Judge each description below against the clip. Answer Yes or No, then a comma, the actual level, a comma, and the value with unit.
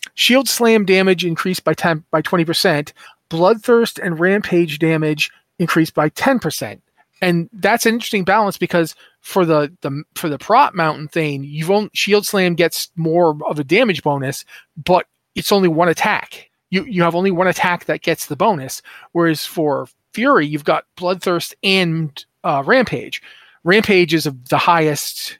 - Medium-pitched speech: Yes, medium, 175 Hz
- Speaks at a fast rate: No, average, 165 wpm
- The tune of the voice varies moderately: Yes, average, 3.6 semitones